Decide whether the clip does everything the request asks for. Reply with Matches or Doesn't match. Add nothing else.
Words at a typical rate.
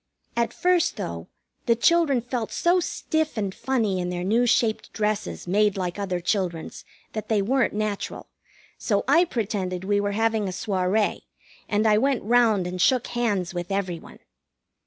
Matches